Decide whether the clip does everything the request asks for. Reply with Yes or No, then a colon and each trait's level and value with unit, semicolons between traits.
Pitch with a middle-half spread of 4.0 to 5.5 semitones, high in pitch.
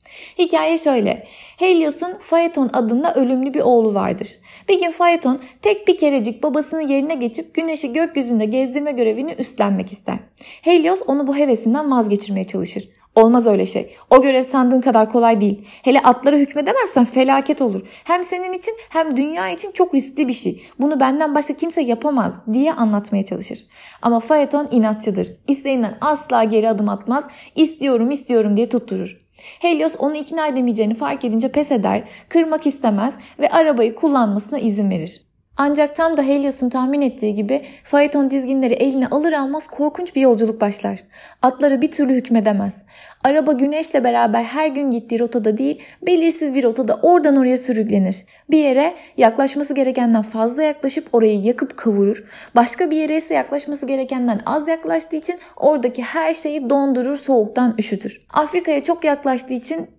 Yes: average, 4.6 semitones; very high, 275 Hz